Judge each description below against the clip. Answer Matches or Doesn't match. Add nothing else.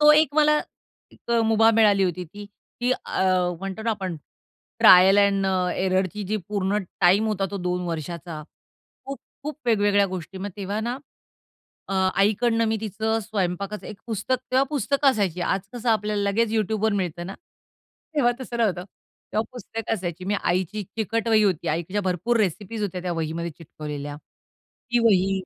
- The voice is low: Doesn't match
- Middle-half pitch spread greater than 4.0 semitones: Doesn't match